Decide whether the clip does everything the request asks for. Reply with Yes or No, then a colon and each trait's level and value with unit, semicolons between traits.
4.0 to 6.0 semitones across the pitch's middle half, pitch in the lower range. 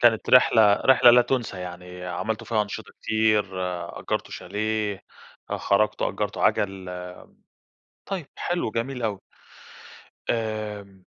No: average, 3.0 semitones; low, 110 Hz